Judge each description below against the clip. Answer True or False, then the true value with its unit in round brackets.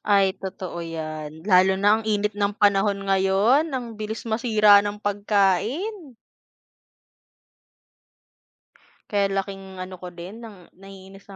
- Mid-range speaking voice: False (200 Hz)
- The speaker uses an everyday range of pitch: False (2.0 semitones)